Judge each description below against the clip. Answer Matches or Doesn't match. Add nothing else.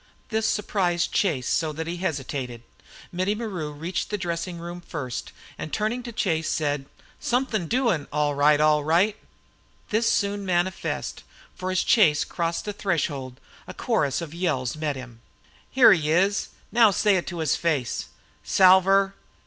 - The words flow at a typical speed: Matches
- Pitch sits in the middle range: Matches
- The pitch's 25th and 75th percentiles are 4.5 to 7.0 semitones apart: Matches